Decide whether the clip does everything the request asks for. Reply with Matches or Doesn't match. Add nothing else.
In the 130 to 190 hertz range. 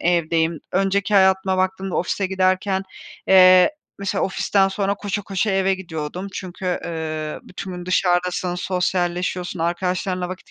Matches